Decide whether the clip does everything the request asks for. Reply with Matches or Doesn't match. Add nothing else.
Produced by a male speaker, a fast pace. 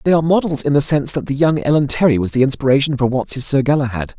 Matches